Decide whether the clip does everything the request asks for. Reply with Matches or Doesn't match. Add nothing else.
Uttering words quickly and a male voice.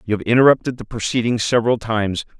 Doesn't match